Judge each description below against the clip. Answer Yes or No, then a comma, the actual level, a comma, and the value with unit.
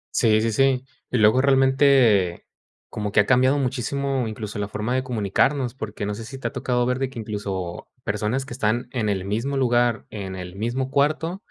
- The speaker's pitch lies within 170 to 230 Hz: No, low, 120 Hz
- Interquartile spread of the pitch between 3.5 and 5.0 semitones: Yes, average, 4.0 semitones